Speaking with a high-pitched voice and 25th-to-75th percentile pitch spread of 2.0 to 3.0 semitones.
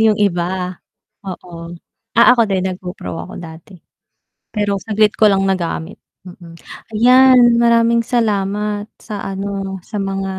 Yes: high, 200 Hz; average, 2.7 semitones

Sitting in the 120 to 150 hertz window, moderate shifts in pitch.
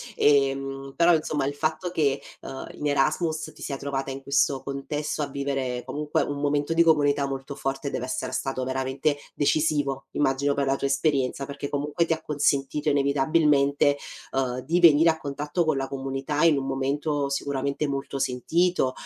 No: medium, 140 Hz; narrow, 1.7 semitones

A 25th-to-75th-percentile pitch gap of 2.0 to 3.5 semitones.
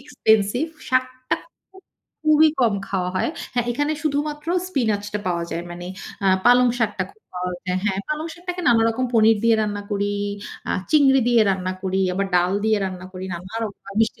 No: wide, 5.4 semitones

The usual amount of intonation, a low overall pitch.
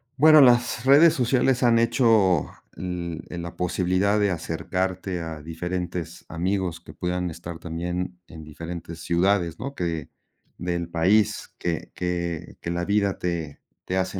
Yes: average, 3.0 semitones; very low, 90 Hz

